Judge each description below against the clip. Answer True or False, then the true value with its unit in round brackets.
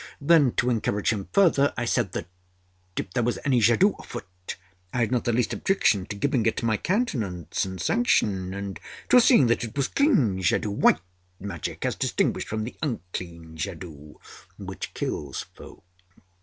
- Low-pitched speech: True (110 Hz)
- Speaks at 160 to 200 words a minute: True (170 wpm)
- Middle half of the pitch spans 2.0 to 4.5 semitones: False (5.6 semitones)